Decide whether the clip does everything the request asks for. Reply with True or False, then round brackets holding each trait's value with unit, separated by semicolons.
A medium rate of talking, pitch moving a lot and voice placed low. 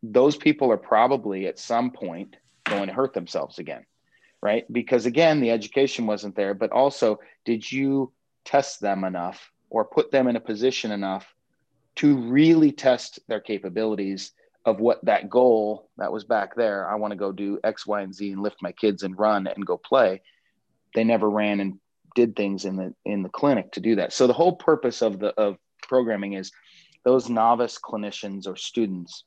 False (190 wpm; 4.2 semitones; 110 Hz)